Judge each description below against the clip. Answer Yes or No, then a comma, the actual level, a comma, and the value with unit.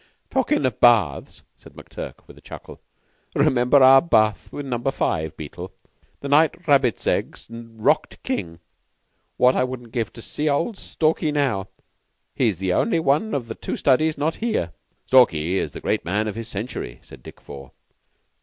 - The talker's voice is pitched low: Yes, low, 125 Hz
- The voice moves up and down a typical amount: No, wide, 5.7 semitones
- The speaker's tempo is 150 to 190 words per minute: Yes, average, 170 wpm